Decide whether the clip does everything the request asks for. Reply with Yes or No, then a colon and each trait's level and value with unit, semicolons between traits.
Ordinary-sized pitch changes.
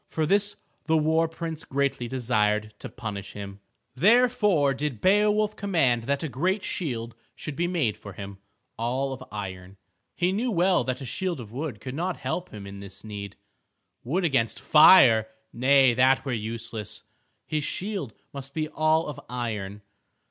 No: wide, 6.9 semitones